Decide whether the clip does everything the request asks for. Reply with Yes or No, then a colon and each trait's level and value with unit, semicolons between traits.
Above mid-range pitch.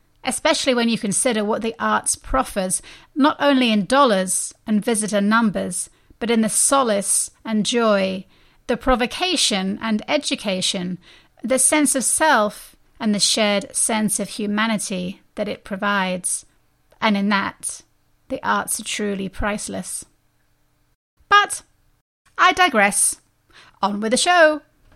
Yes: high, 220 Hz